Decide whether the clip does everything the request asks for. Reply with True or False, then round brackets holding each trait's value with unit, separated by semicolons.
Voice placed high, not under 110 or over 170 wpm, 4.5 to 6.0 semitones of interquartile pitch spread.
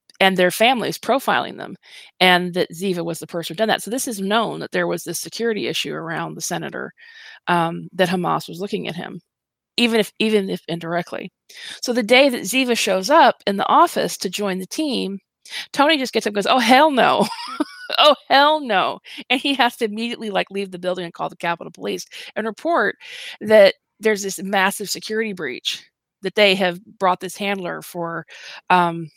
False (200 Hz; 195 wpm; 5.5 semitones)